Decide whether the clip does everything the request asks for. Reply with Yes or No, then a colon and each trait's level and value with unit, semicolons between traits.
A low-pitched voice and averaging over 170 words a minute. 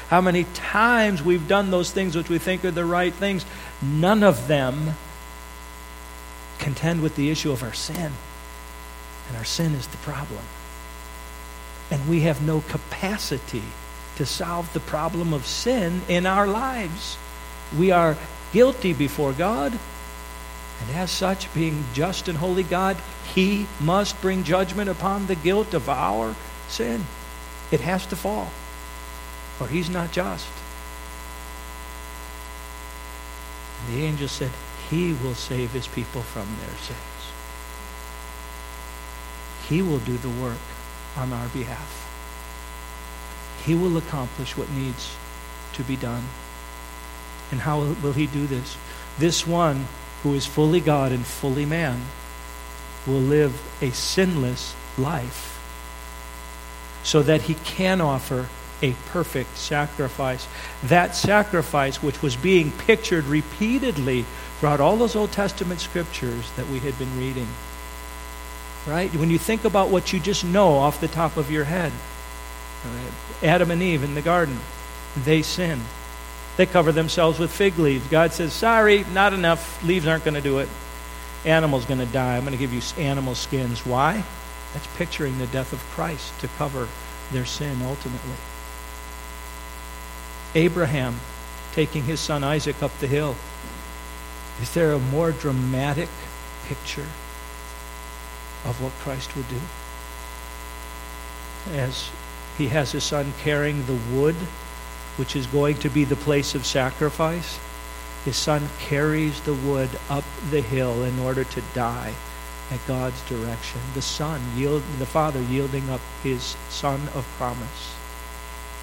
No: low, 130 Hz; average, 140 wpm